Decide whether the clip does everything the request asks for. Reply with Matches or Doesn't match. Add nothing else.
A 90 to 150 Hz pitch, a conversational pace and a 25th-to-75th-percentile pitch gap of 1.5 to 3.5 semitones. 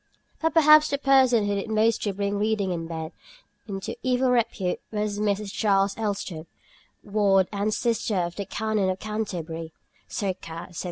Doesn't match